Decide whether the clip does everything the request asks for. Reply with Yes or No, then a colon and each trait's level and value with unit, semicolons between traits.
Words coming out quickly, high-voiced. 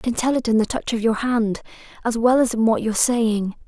Yes: fast, 275 wpm; high, 230 Hz